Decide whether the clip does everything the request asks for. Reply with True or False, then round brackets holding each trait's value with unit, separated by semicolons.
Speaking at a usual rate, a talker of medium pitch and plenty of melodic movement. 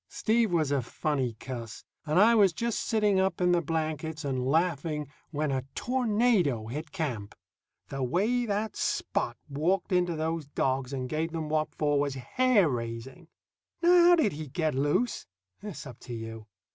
True (170 wpm; 155 Hz; 6.1 semitones)